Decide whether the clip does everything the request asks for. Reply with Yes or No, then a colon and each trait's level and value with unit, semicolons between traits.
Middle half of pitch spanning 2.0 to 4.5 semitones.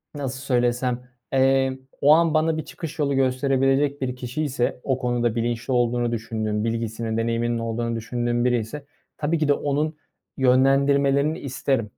Yes: average, 2.9 semitones